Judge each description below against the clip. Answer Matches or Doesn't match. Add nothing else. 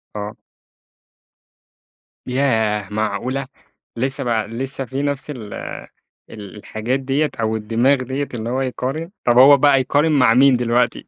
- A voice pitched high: Doesn't match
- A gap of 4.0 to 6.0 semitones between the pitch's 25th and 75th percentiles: Doesn't match